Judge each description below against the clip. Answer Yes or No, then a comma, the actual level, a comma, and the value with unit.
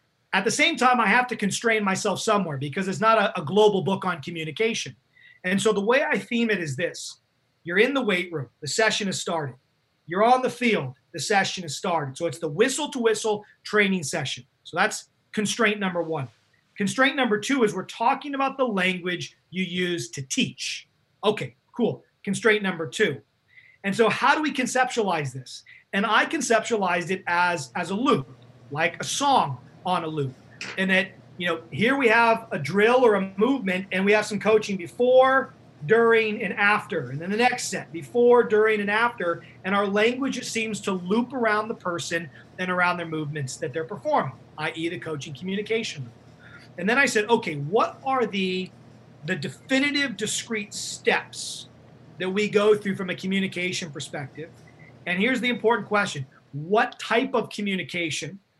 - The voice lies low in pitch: No, high, 190 Hz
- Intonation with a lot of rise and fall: Yes, wide, 5.8 semitones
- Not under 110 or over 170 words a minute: No, average, 180 wpm